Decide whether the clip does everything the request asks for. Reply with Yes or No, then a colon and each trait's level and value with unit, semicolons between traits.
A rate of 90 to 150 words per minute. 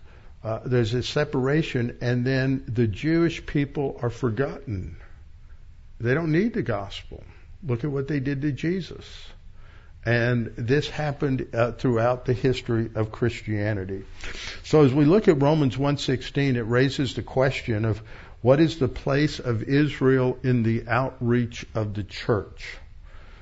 Yes: average, 145 wpm